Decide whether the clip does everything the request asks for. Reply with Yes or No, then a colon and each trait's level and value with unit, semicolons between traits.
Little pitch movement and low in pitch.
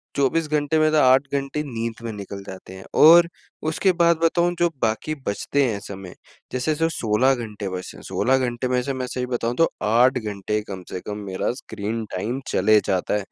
No: wide, 5.4 semitones; low, 120 Hz